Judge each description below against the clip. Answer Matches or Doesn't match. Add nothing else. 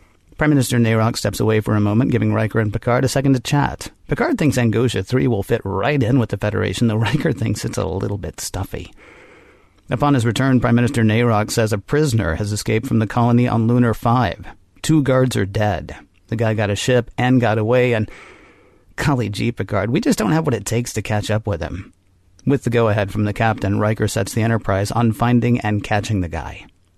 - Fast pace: Matches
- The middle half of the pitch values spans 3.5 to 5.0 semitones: Doesn't match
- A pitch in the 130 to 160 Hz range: Doesn't match